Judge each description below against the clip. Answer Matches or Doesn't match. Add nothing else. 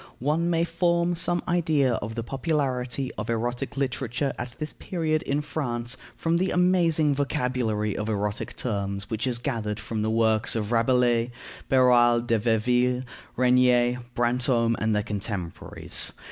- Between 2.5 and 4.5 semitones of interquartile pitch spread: Matches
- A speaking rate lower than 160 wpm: Matches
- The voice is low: Matches